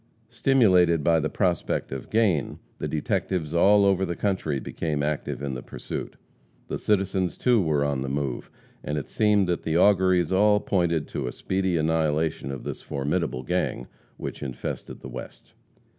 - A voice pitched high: No, very low, 85 Hz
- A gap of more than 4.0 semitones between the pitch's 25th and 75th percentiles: Yes, average, 4.8 semitones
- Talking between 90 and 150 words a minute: No, average, 165 wpm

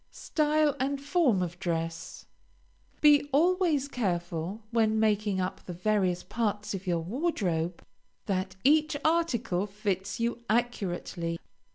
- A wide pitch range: Yes, wide, 7.6 semitones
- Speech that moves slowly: Yes, slow, 120 wpm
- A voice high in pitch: Yes, high, 210 Hz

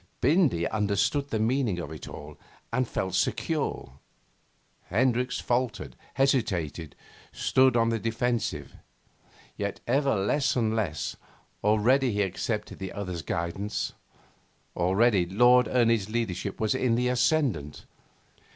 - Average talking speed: No, slow, 115 wpm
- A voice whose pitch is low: Yes, low, 115 Hz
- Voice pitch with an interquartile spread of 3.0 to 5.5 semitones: Yes, average, 4.8 semitones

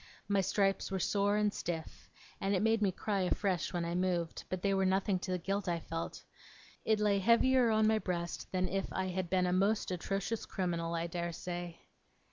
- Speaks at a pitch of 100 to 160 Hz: No, high, 190 Hz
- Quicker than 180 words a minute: Yes, average, 200 wpm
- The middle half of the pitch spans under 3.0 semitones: Yes, narrow, 2.4 semitones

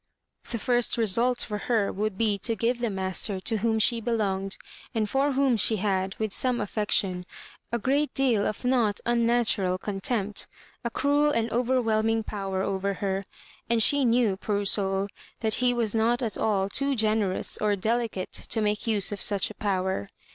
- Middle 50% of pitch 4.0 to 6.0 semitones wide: No, average, 3.2 semitones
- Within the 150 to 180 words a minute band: Yes, average, 175 wpm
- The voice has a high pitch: Yes, high, 220 Hz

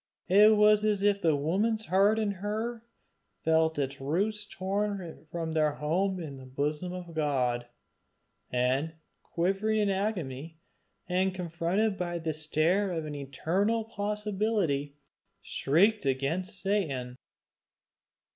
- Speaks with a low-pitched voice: No, medium, 180 Hz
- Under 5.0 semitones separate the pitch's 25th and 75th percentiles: No, average, 5.3 semitones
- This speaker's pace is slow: Yes, slow, 120 wpm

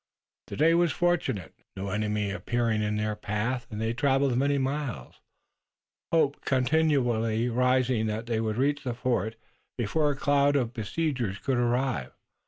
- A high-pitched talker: No, low, 120 Hz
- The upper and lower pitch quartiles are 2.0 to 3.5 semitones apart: No, average, 4.4 semitones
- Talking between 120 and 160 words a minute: Yes, average, 150 wpm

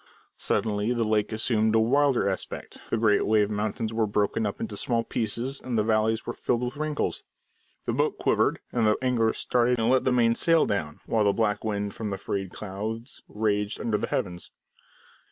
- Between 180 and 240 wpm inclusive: Yes, average, 190 wpm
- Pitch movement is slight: Yes, narrow, 2.2 semitones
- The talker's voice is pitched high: No, low, 110 Hz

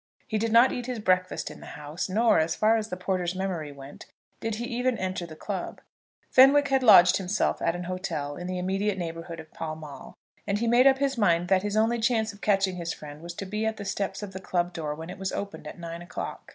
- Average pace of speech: No, fast, 245 wpm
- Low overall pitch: No, high, 190 Hz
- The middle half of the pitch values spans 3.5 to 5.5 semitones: Yes, average, 4.4 semitones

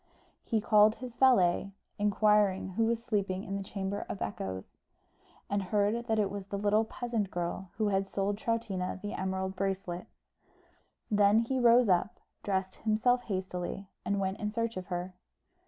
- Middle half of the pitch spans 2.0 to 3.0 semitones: Yes, narrow, 2.6 semitones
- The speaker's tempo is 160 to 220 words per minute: Yes, average, 165 wpm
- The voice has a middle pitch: No, high, 200 Hz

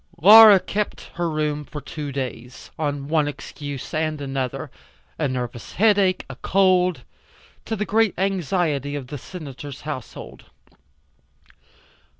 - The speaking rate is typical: No, slow, 125 wpm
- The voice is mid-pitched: Yes, medium, 150 Hz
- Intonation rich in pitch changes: No, average, 4.8 semitones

